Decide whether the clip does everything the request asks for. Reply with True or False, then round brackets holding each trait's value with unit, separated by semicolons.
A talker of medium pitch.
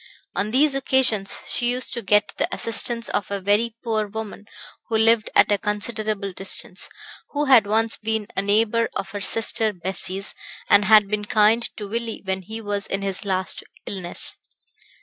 False (210 Hz)